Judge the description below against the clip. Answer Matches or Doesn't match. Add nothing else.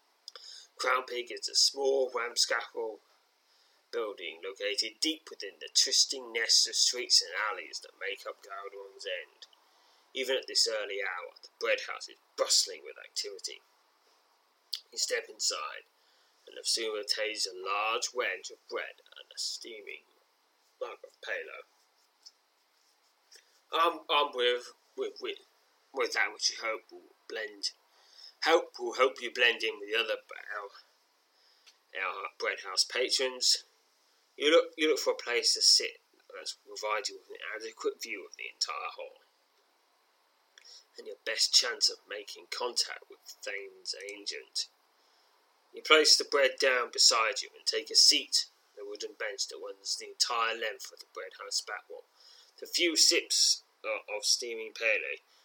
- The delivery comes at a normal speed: Matches